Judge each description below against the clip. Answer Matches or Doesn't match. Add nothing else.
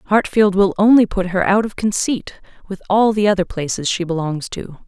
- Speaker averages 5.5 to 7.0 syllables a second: Doesn't match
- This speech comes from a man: Doesn't match